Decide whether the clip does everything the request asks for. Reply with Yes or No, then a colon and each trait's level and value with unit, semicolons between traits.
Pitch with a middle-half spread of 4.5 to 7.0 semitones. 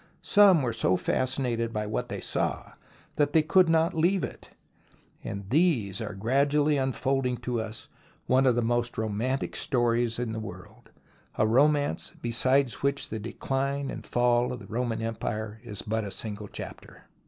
No: average, 3.8 semitones